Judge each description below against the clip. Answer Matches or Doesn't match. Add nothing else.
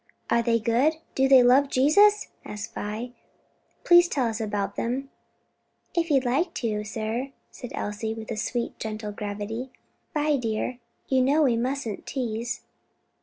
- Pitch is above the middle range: Matches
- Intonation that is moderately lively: Matches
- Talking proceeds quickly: Doesn't match